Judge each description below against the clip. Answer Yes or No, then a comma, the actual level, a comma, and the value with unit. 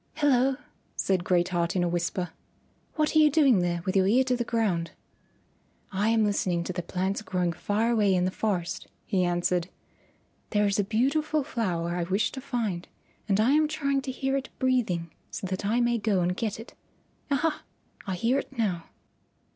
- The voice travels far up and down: Yes, wide, 6.0 semitones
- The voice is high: Yes, high, 205 Hz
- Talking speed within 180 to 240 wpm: Yes, average, 190 wpm